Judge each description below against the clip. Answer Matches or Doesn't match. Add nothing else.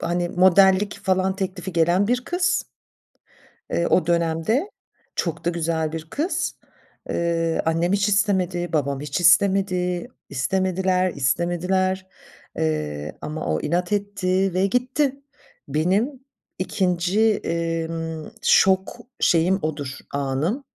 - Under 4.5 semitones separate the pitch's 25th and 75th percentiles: Matches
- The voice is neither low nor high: Matches